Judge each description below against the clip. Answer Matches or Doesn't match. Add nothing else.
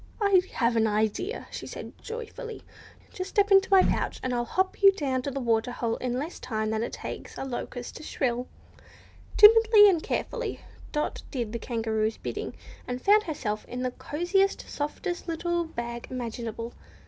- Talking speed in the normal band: Matches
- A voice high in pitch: Matches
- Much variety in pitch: Matches